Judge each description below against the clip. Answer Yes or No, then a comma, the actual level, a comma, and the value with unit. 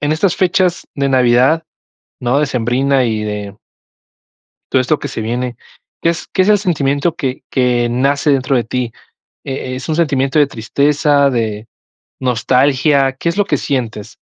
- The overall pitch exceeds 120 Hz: Yes, low, 135 Hz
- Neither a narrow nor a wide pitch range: Yes, average, 3.3 semitones